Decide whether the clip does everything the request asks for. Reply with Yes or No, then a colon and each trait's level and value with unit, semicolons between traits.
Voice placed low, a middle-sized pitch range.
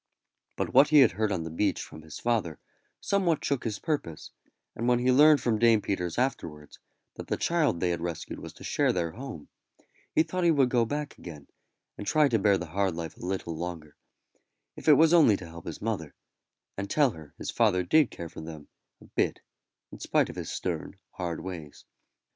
No: low, 100 Hz; wide, 8.2 semitones